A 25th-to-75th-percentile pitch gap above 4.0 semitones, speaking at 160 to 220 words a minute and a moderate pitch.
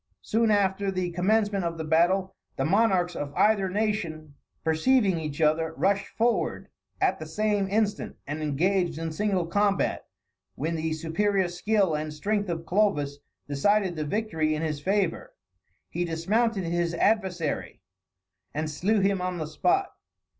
No: average, 4.4 semitones; average, 145 wpm; medium, 180 Hz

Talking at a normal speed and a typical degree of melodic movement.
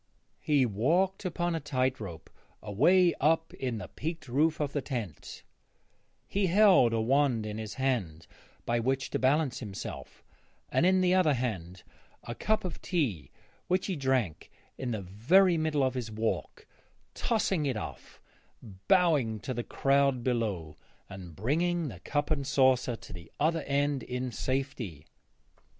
No: average, 155 wpm; wide, 6.3 semitones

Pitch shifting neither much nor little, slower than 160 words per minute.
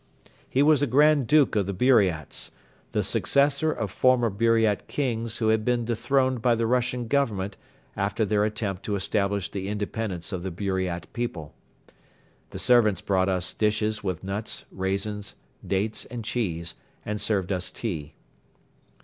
Yes: average, 3.8 semitones; average, 150 wpm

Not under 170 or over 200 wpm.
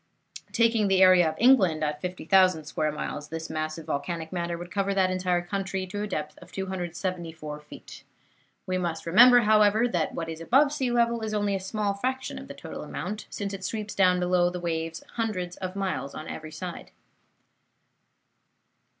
Yes: average, 180 wpm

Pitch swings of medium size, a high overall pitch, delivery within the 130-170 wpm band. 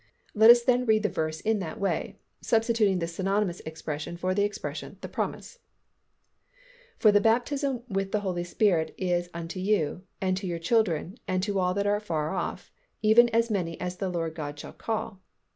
No: average, 4.0 semitones; high, 195 Hz; average, 185 wpm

